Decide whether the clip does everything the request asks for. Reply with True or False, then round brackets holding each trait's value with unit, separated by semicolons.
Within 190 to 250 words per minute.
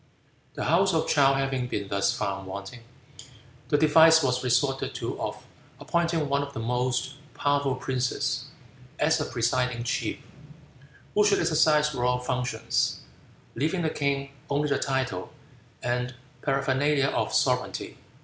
False (135 wpm)